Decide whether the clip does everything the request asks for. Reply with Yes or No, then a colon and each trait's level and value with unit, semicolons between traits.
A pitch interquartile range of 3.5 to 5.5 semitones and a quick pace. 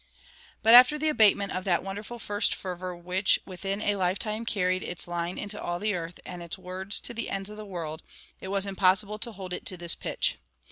No: narrow, 2.6 semitones; fast, 220 wpm